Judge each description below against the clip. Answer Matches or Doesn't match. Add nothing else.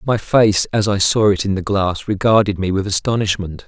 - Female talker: Doesn't match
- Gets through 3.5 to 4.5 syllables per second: Doesn't match